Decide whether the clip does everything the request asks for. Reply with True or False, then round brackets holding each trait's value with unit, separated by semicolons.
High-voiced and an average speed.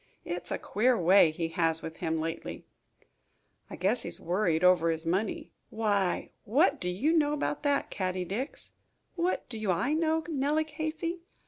True (205 Hz; 175 wpm)